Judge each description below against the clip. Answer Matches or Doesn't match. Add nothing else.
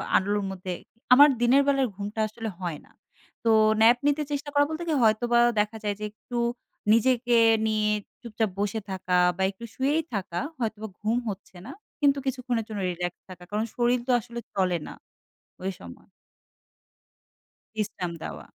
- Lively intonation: Doesn't match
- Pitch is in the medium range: Doesn't match